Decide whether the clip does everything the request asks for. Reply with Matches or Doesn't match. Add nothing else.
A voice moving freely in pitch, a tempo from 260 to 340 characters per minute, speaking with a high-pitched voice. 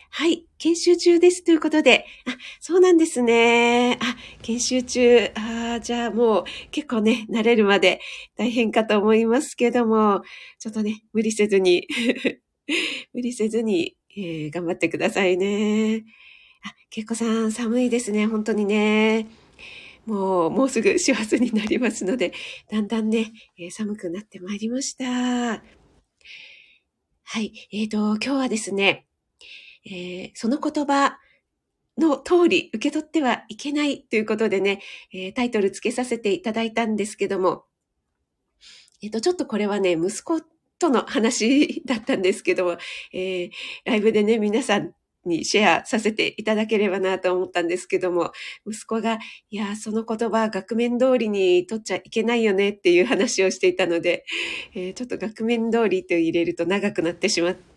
Doesn't match